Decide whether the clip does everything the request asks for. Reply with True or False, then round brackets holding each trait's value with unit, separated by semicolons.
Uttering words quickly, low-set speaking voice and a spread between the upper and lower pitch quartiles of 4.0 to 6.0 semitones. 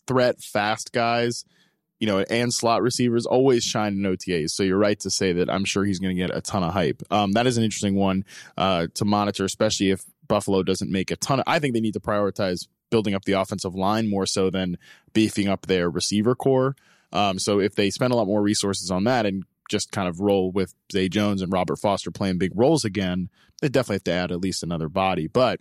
False (235 wpm; 100 Hz; 2.7 semitones)